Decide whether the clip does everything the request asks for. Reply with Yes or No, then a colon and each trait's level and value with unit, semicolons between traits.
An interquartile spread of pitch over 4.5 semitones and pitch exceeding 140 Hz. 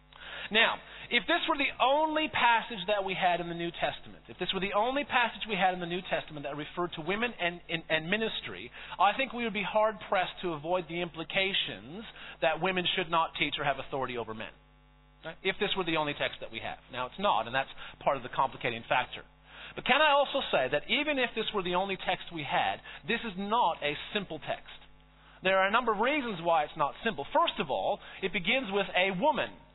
Yes: wide, 5.6 semitones; high, 190 Hz